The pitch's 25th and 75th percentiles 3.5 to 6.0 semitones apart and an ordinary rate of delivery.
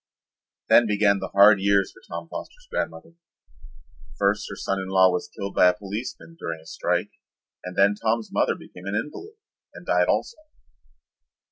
No: narrow, 2.4 semitones; average, 165 wpm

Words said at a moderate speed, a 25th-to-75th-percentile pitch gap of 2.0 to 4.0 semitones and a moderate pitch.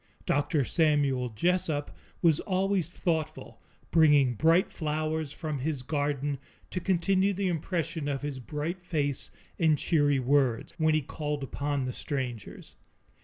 No: slow, 130 wpm; average, 2.9 semitones; medium, 150 Hz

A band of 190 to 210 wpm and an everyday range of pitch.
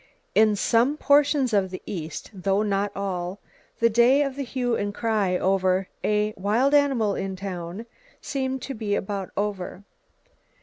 No: average, 150 wpm; average, 4.1 semitones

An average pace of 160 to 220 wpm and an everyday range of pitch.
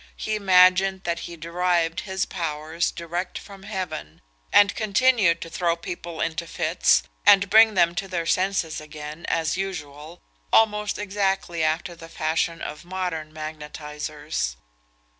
No: slow, 135 wpm; average, 3.4 semitones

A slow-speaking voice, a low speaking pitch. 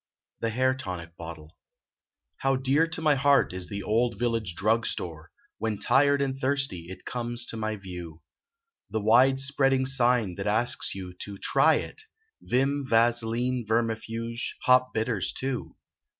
No: average, 150 wpm; low, 115 Hz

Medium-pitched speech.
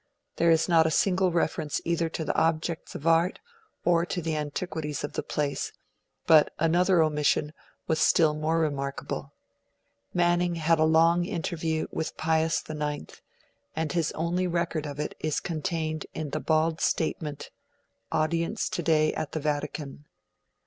Yes: medium, 160 Hz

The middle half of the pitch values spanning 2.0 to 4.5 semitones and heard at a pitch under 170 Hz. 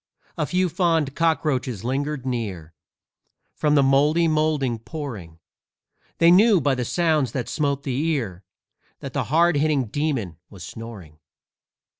No: average, 5.1 semitones; medium, 140 Hz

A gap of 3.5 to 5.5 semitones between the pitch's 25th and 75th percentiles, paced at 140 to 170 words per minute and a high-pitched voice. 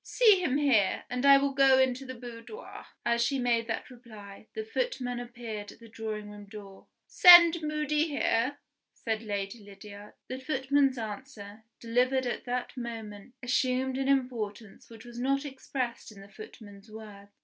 Yes: average, 3.9 semitones; average, 160 wpm; high, 245 Hz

